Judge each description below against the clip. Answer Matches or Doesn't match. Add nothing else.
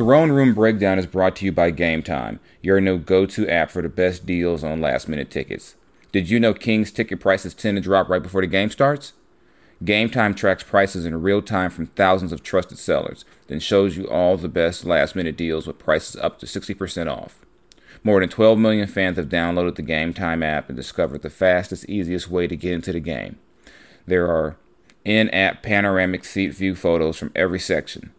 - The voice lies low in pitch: Matches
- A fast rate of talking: Doesn't match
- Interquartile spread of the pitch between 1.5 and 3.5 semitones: Matches